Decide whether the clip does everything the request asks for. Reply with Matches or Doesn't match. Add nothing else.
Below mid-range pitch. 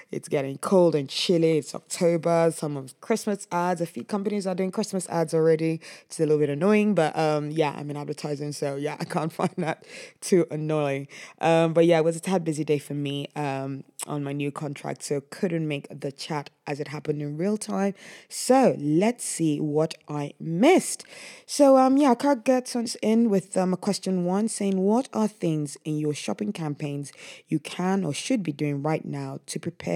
Doesn't match